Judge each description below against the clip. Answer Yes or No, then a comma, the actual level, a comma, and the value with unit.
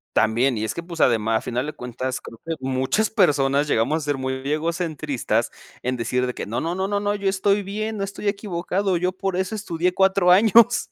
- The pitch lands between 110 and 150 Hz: No, medium, 170 Hz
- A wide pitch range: Yes, wide, 7.0 semitones